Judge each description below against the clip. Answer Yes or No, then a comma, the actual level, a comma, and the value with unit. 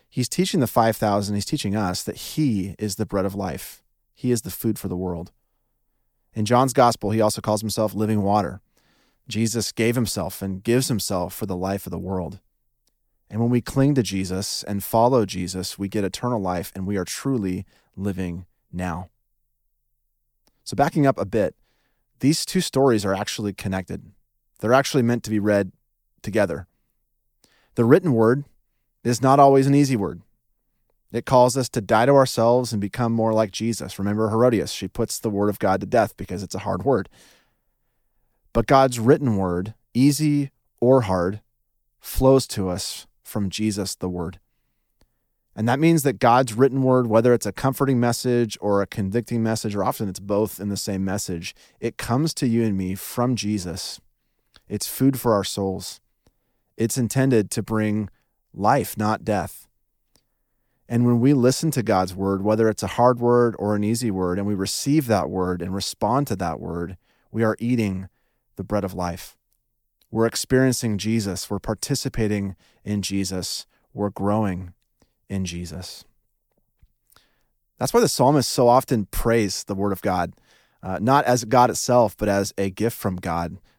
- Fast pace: No, average, 170 wpm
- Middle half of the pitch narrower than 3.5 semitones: No, average, 3.8 semitones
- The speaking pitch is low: Yes, low, 110 Hz